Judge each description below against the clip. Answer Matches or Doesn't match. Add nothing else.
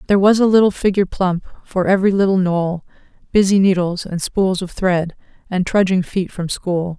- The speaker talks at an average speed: Matches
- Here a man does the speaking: Doesn't match